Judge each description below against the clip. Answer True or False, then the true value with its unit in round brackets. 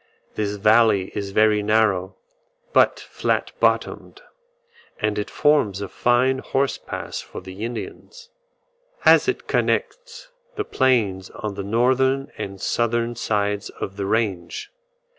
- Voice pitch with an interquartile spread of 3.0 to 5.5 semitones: True (4.2 semitones)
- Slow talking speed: True (125 wpm)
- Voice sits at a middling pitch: False (110 Hz)